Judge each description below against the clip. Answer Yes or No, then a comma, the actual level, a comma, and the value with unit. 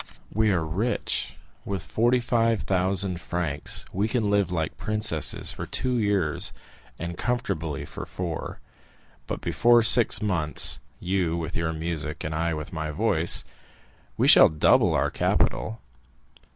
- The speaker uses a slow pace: Yes, slow, 130 wpm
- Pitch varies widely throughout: No, average, 5.0 semitones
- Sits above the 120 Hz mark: No, very low, 90 Hz